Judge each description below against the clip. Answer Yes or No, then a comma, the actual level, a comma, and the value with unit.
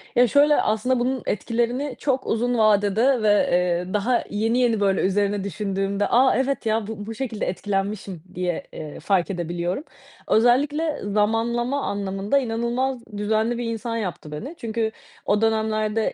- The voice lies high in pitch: Yes, high, 220 Hz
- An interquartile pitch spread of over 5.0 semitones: No, average, 3.2 semitones